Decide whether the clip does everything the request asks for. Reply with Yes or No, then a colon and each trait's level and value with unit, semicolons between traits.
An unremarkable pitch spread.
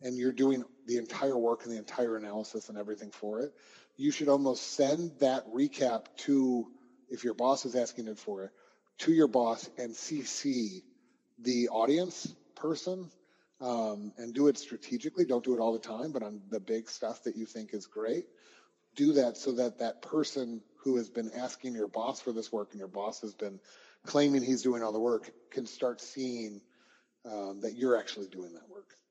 Yes: average, 4.0 semitones